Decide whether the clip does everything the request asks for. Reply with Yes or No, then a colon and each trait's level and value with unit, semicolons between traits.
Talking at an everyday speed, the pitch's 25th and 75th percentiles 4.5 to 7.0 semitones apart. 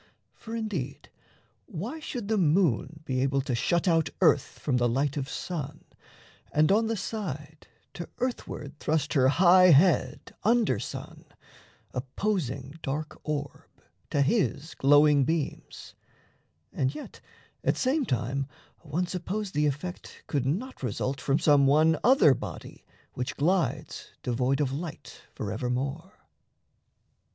No: slow, 130 wpm; average, 5.1 semitones